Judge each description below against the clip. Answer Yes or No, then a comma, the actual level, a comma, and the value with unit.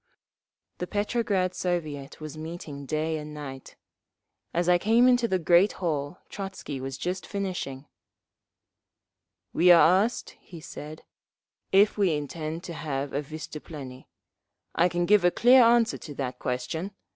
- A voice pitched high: No, medium, 170 Hz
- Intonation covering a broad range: No, average, 4.3 semitones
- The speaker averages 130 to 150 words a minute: Yes, average, 140 wpm